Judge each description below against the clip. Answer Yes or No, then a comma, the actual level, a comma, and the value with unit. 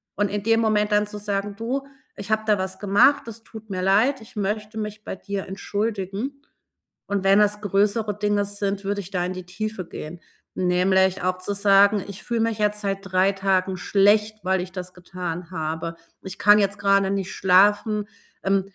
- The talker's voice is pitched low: No, high, 200 Hz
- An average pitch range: No, narrow, 1.8 semitones